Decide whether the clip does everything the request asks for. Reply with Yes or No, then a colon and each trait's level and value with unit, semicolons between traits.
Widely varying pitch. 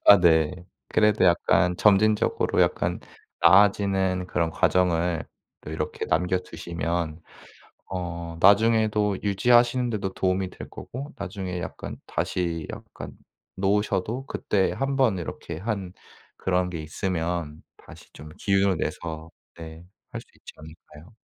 No: average, 3.4 semitones